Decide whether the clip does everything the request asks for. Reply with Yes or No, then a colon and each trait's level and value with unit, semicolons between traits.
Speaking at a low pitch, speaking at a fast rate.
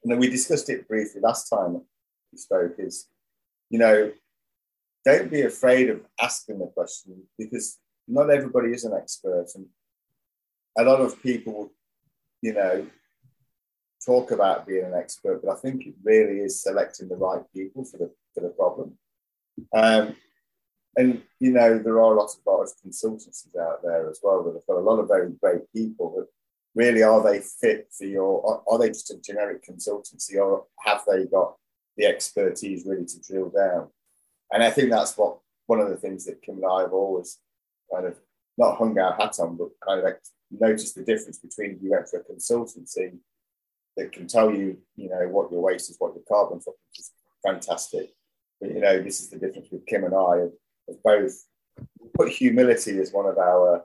No: low, 120 Hz; average, 195 wpm